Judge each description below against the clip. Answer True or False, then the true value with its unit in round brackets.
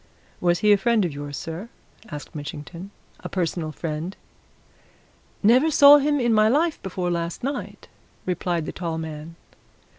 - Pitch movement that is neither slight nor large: False (6.2 semitones)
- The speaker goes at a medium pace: True (150 wpm)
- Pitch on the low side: False (180 Hz)